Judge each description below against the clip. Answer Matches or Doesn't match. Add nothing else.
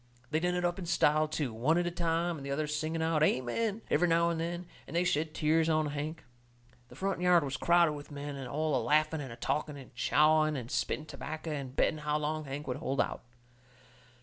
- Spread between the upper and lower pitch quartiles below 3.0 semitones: Matches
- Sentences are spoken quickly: Matches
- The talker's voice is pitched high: Doesn't match